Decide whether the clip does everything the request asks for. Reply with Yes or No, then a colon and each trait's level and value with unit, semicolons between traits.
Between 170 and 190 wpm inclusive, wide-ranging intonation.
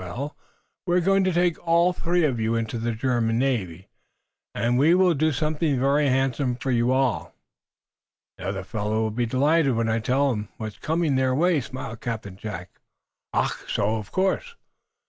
Yes: average, 180 wpm; wide, 5.7 semitones